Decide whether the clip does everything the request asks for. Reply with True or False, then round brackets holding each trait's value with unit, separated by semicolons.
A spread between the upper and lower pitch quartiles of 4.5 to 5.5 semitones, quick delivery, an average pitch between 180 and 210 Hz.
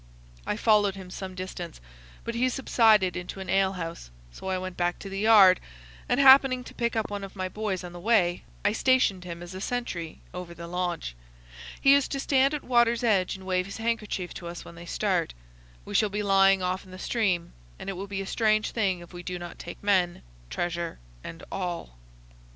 False (3.6 semitones; 215 wpm; 190 Hz)